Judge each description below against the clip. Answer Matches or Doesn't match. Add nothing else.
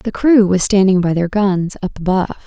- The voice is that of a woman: Matches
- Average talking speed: Doesn't match